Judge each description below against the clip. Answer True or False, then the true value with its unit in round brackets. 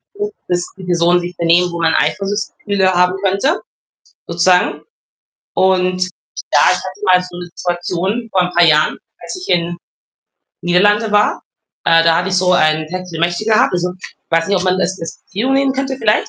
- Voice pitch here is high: False (180 Hz)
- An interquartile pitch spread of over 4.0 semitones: False (2.7 semitones)